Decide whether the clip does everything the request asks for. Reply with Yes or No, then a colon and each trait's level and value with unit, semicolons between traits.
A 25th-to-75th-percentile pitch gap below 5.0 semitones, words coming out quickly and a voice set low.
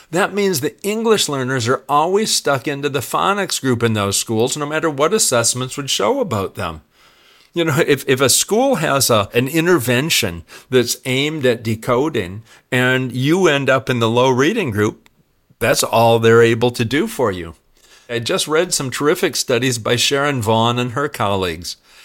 No: average, 4.5 semitones; average, 180 wpm; low, 130 Hz